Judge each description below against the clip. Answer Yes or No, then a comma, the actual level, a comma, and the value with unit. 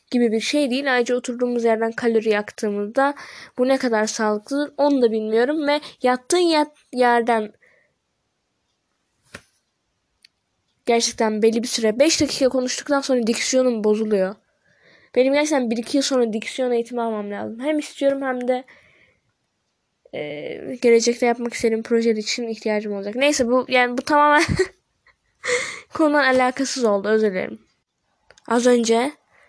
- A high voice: Yes, high, 245 Hz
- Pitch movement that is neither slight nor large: Yes, average, 3.4 semitones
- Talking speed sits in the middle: Yes, average, 130 wpm